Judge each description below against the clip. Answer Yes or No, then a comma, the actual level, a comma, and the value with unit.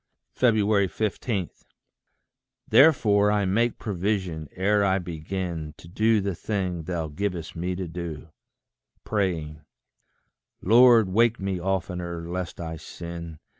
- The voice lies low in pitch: Yes, very low, 95 Hz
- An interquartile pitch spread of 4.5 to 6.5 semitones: No, average, 3.5 semitones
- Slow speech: Yes, slow, 110 wpm